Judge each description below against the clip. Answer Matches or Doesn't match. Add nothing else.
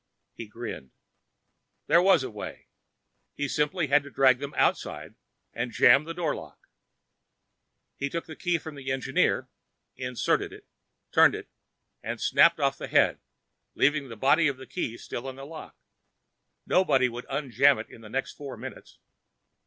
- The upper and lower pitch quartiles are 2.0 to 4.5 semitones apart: Matches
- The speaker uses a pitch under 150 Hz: Matches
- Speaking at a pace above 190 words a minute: Doesn't match